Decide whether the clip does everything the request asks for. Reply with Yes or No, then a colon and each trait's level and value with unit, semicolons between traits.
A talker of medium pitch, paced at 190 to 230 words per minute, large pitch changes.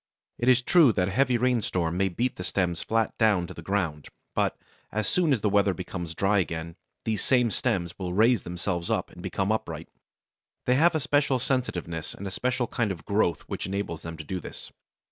No: low, 100 Hz; fast, 205 wpm; wide, 5.8 semitones